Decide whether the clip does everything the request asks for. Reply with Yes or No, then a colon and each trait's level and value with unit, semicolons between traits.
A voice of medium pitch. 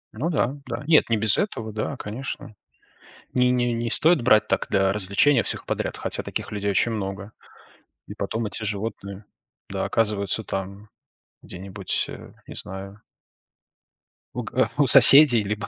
No: low, 110 Hz